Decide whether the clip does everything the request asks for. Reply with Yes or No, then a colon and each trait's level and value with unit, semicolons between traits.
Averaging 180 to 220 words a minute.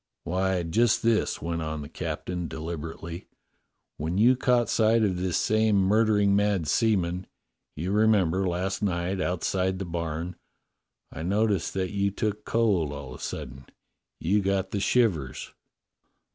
No: average, 150 wpm